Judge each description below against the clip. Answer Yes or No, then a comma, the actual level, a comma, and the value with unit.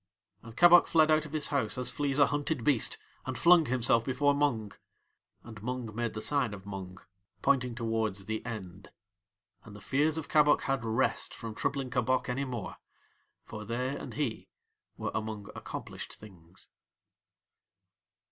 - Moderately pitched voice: No, low, 125 Hz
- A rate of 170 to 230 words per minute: No, average, 155 wpm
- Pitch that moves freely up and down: No, average, 4.6 semitones